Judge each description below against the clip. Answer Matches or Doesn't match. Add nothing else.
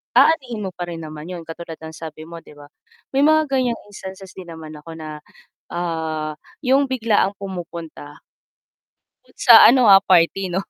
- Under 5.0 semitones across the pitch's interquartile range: Doesn't match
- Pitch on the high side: Doesn't match